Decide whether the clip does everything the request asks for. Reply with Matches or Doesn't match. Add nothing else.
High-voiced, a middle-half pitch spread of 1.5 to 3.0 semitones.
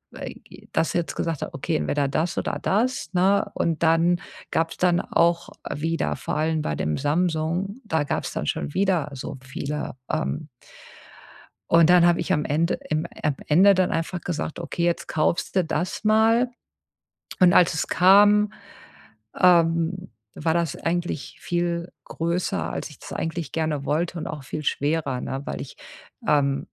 Doesn't match